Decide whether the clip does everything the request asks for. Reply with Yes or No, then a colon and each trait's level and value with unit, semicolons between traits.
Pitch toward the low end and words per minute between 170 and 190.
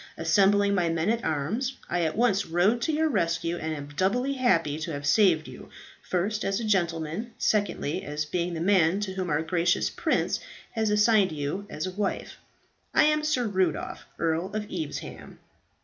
No: medium, 185 Hz; average, 180 wpm